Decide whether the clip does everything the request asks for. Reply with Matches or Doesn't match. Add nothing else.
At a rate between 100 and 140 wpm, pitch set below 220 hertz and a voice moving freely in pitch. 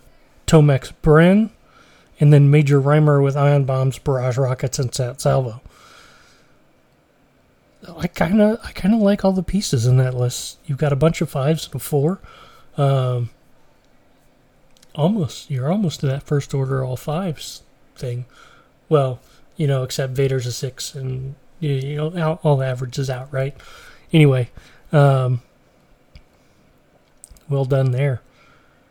Doesn't match